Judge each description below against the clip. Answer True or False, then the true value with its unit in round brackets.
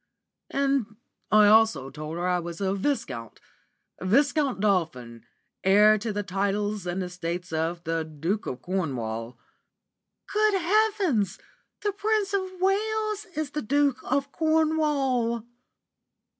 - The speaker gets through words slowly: True (120 wpm)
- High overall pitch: True (215 Hz)